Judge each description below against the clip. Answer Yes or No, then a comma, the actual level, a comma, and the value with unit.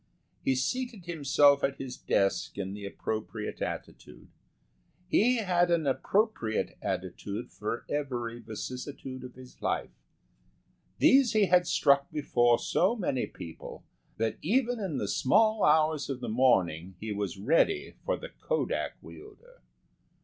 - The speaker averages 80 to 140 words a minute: Yes, slow, 135 wpm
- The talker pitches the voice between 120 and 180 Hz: Yes, medium, 140 Hz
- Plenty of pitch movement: Yes, wide, 8.8 semitones